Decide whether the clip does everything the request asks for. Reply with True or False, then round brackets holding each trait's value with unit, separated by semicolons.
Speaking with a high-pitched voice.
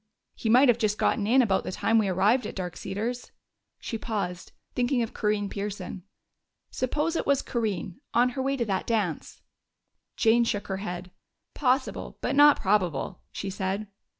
True (215 Hz)